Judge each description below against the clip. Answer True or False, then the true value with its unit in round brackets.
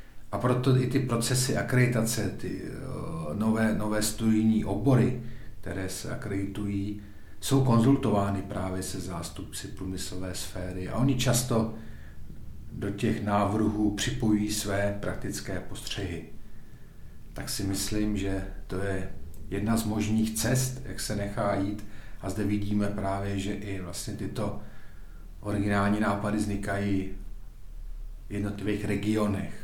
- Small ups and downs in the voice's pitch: True (2.3 semitones)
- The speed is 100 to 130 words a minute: True (120 wpm)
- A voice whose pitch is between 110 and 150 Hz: False (100 Hz)